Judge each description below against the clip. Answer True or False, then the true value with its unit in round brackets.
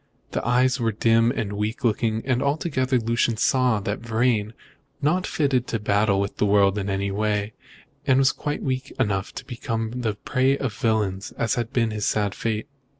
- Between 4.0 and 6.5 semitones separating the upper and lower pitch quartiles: False (3.6 semitones)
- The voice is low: True (115 Hz)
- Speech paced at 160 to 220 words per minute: True (185 wpm)